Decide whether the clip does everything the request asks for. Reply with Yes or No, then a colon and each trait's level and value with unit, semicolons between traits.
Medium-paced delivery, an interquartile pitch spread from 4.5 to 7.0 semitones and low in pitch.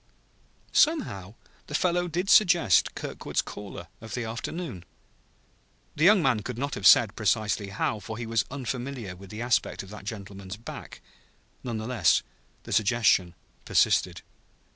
Yes: average, 145 wpm; average, 5.2 semitones; low, 115 Hz